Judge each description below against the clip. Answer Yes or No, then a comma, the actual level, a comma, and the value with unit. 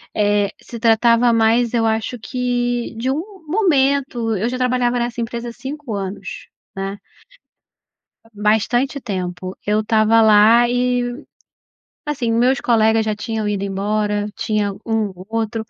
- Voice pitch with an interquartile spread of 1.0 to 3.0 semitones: Yes, narrow, 2.6 semitones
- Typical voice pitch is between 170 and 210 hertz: No, high, 225 Hz